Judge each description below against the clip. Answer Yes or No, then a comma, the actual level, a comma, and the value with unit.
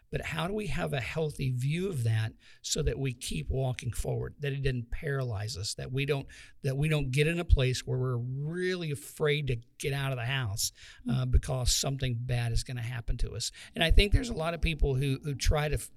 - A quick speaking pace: Yes, fast, 240 wpm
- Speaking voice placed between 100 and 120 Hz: No, low, 135 Hz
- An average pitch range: Yes, average, 3.3 semitones